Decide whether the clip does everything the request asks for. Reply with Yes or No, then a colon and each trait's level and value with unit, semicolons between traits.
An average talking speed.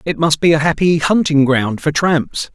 No: fast, 210 wpm